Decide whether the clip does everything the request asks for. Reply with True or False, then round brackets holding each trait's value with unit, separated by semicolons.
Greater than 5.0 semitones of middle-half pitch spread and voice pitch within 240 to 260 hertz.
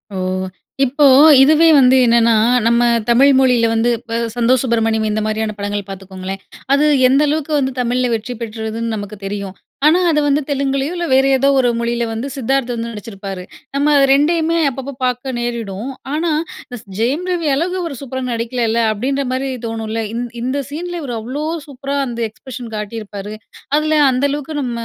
False (3.8 semitones; 245 Hz)